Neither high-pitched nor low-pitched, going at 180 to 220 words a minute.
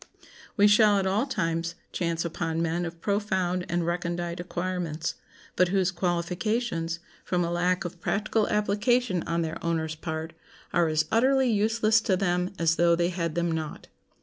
No: medium, 175 Hz; average, 160 wpm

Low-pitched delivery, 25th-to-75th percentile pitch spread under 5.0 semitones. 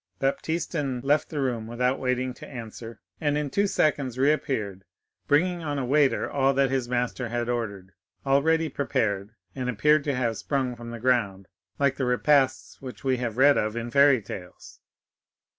Yes: low, 130 Hz; average, 3.3 semitones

